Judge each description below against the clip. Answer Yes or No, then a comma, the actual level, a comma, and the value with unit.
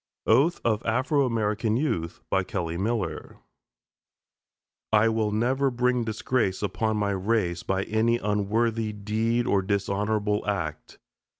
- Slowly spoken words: Yes, slow, 115 wpm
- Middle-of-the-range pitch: No, low, 110 Hz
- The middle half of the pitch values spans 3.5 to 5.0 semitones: No, narrow, 2.6 semitones